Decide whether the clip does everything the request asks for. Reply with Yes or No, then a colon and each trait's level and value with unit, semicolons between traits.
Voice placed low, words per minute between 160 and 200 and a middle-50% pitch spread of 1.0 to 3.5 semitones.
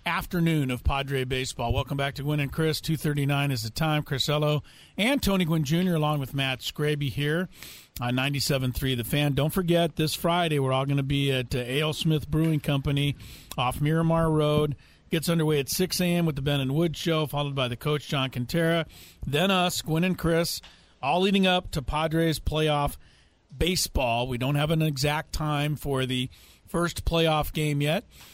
No: medium, 150 Hz; average, 180 wpm; average, 3.2 semitones